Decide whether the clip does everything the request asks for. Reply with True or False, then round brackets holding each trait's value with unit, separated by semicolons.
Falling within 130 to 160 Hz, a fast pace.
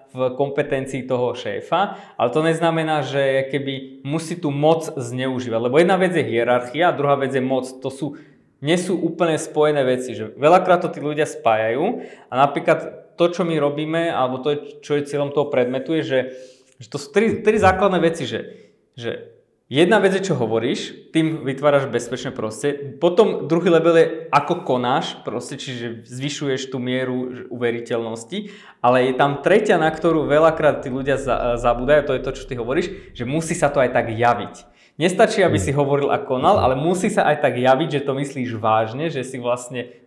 True (140 Hz; 185 wpm)